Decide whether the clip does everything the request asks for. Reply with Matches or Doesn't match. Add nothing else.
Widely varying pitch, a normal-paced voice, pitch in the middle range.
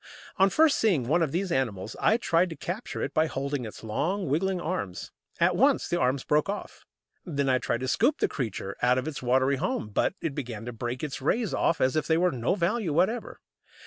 Doesn't match